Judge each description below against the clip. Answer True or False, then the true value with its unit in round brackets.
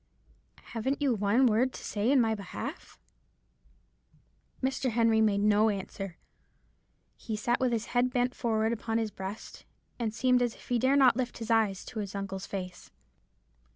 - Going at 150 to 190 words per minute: True (165 wpm)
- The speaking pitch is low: False (225 Hz)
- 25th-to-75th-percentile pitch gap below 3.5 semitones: True (2.9 semitones)